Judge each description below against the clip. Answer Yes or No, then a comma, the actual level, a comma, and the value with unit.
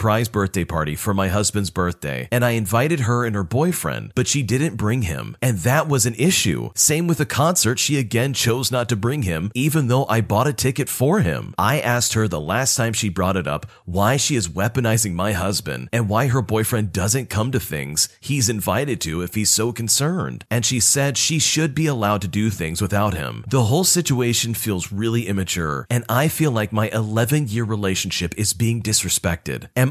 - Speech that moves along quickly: Yes, fast, 210 wpm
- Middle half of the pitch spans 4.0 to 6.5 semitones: Yes, average, 4.4 semitones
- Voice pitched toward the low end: Yes, low, 115 Hz